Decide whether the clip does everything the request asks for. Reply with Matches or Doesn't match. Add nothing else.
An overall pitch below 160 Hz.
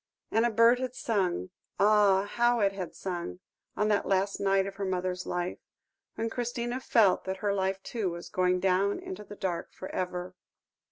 Doesn't match